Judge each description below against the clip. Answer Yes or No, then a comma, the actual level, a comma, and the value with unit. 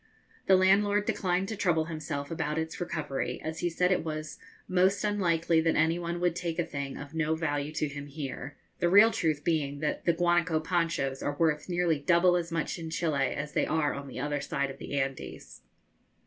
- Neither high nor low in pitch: Yes, medium, 160 Hz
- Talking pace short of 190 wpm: No, fast, 205 wpm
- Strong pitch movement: No, average, 3.0 semitones